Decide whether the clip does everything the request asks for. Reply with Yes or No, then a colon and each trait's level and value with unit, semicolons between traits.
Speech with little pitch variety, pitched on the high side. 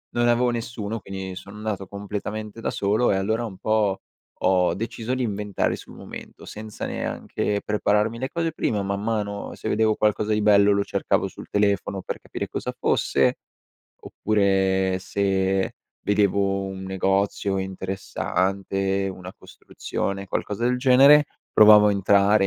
No: narrow, 1.9 semitones; low, 100 Hz